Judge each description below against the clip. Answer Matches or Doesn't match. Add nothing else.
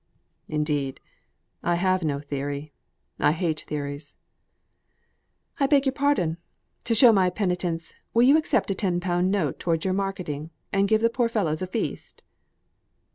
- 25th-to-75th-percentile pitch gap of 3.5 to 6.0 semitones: Matches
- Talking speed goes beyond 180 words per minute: Doesn't match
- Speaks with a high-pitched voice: Doesn't match